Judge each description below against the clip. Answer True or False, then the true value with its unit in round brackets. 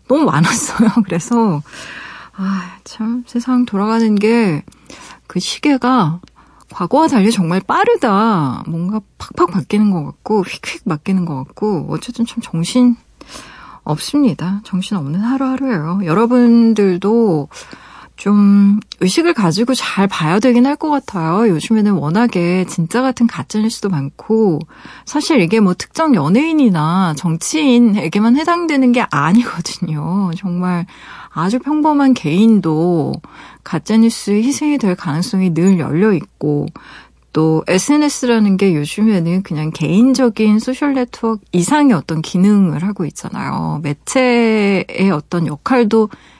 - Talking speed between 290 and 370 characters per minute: False (275 characters per minute)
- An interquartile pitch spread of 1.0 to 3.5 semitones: False (5.4 semitones)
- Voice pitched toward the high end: True (205 Hz)